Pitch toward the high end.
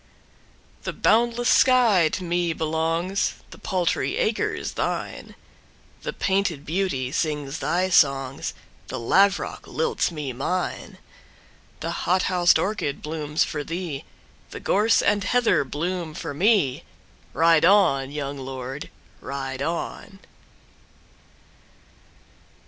No: medium, 165 Hz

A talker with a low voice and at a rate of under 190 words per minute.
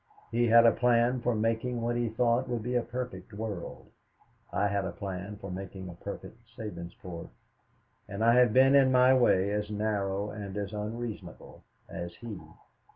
Yes: low, 110 Hz; average, 170 wpm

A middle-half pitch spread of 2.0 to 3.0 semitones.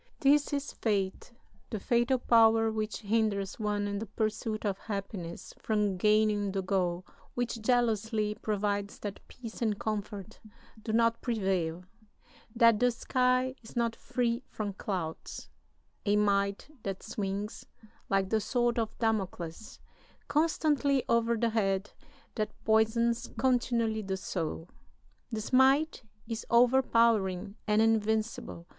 Yes: average, 2.7 semitones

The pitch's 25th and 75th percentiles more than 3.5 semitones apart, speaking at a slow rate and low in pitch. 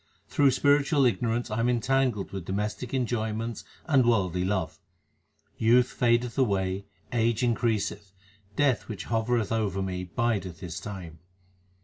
Yes: average, 4.0 semitones; slow, 130 wpm; low, 115 Hz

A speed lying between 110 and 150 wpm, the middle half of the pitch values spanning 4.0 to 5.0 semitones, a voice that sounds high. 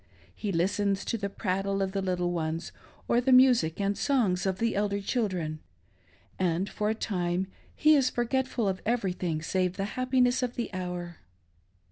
No: average, 165 wpm; average, 4.5 semitones; high, 195 Hz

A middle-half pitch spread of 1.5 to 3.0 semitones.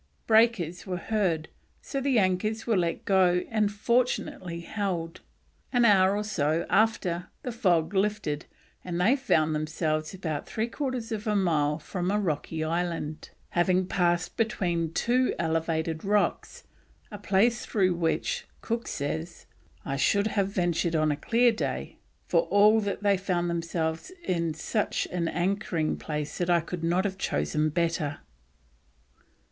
No: average, 4.3 semitones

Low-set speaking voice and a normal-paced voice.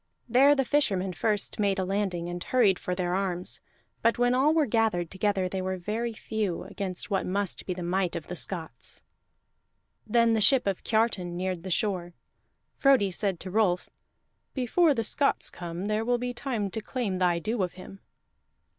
No: high, 200 Hz; average, 180 wpm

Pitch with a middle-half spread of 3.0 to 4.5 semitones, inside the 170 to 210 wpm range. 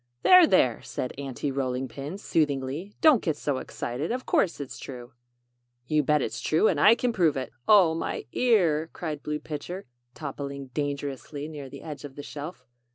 Yes: average, 3.8 semitones; average, 175 wpm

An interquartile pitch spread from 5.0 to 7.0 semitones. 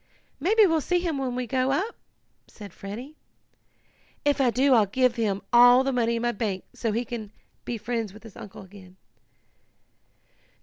No: average, 3.9 semitones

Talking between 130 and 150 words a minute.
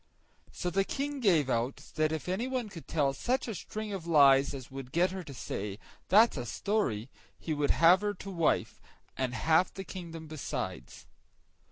No: average, 180 wpm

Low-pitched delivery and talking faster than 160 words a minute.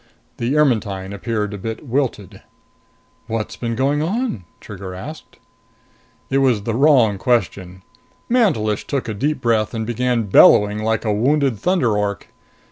No: low, 115 Hz; average, 140 wpm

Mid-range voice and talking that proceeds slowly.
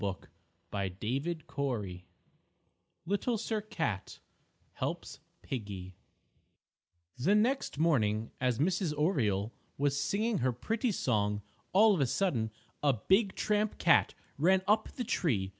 Yes: medium, 150 Hz; slow, 120 wpm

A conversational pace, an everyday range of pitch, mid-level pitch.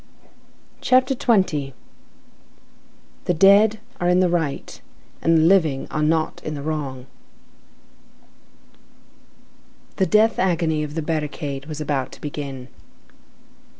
No: slow, 110 wpm; average, 4.1 semitones; medium, 160 Hz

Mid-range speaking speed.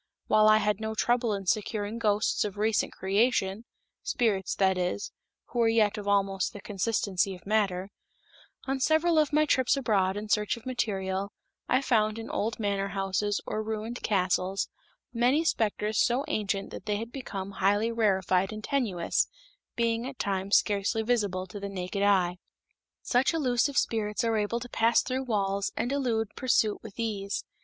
Yes: average, 165 wpm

